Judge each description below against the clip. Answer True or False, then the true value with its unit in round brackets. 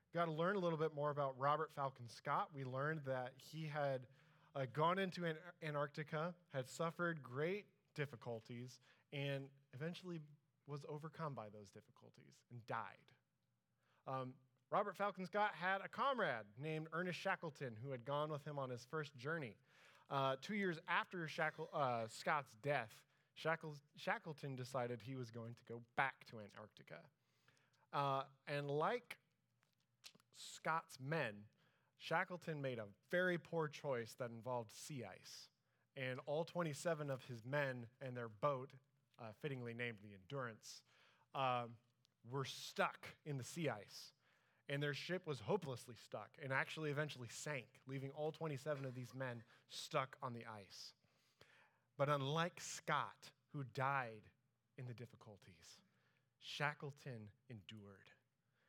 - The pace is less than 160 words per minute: True (140 wpm)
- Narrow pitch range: False (4.0 semitones)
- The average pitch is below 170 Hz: True (140 Hz)